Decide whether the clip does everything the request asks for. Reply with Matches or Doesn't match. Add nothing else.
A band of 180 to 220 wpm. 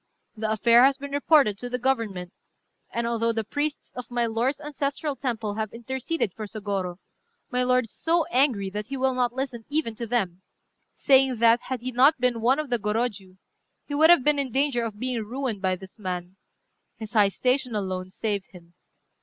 Matches